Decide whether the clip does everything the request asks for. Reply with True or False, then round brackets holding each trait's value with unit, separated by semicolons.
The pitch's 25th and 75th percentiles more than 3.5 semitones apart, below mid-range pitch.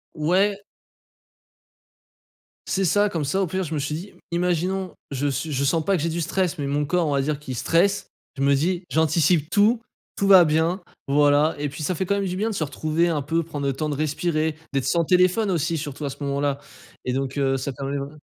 False (4.0 semitones; 155 Hz)